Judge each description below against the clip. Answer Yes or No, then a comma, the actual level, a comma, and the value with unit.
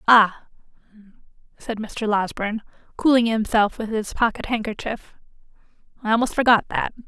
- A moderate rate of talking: No, slow, 120 wpm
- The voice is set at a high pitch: Yes, high, 220 Hz